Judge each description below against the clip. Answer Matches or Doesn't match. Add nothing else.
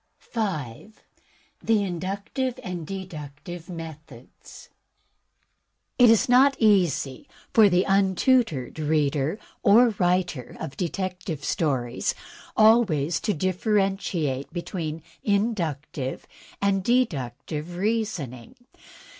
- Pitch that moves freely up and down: Matches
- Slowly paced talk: Matches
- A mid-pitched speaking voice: Matches